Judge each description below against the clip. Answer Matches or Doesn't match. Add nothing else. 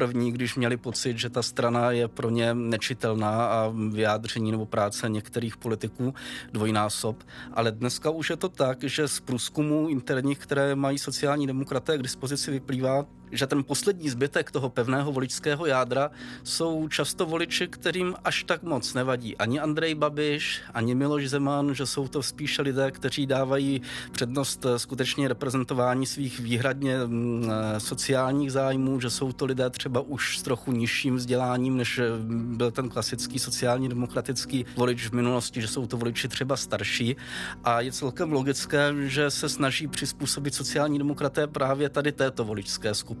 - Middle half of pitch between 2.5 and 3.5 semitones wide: Matches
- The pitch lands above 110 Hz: Matches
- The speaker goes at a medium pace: Matches